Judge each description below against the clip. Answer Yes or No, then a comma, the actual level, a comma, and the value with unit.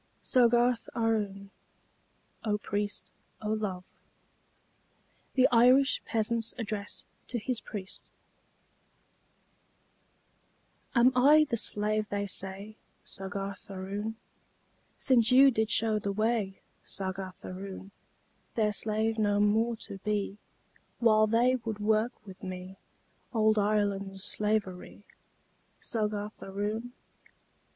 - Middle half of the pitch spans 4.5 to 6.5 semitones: No, narrow, 2.4 semitones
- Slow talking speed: Yes, slow, 100 wpm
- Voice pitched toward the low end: No, high, 215 Hz